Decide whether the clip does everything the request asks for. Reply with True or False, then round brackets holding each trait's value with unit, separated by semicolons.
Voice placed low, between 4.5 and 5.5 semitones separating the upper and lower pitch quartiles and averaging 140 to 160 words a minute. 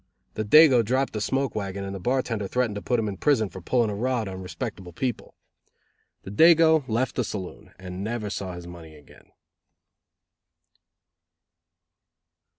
True (110 Hz; 4.9 semitones; 155 wpm)